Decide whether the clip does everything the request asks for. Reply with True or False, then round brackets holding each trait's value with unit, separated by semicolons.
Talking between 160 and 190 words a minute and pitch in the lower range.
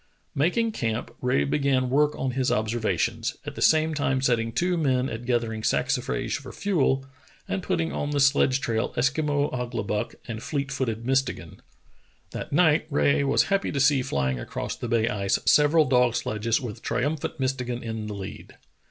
True (170 wpm; 130 Hz)